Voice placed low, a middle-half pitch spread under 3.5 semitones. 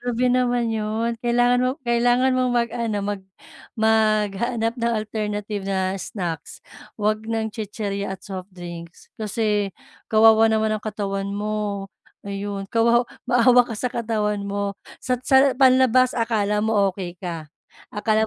No: high, 215 Hz; average, 2.8 semitones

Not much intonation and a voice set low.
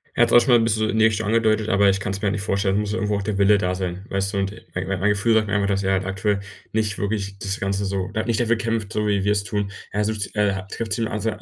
Yes: narrow, 1.7 semitones; low, 100 Hz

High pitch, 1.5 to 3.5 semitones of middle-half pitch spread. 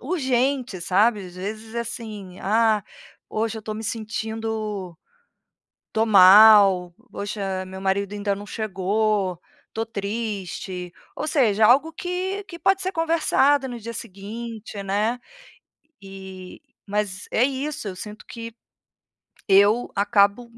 Yes: high, 215 Hz; average, 3.1 semitones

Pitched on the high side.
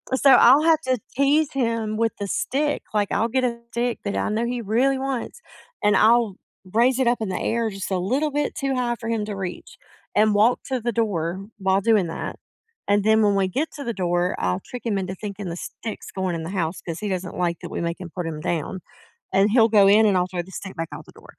Yes: high, 215 Hz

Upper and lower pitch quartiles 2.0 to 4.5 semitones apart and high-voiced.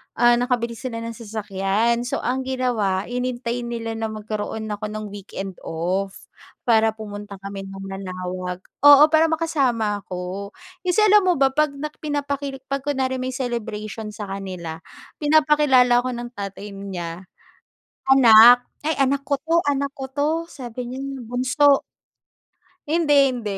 No: average, 4.9 semitones; high, 240 Hz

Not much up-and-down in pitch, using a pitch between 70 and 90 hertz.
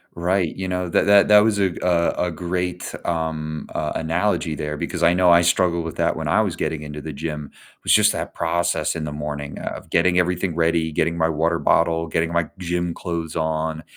Yes: narrow, 1.8 semitones; very low, 85 Hz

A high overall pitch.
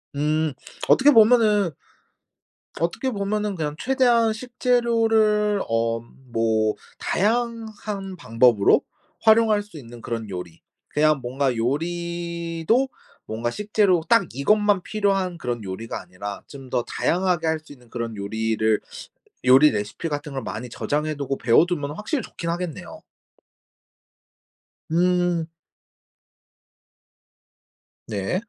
No: medium, 165 Hz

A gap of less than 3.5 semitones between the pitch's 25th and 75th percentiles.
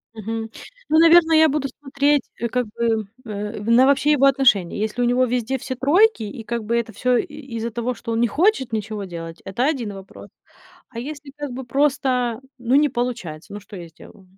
No: average, 4.1 semitones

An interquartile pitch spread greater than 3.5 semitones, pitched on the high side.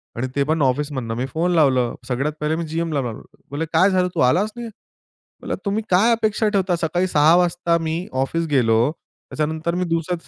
No: average, 4.2 semitones; medium, 160 Hz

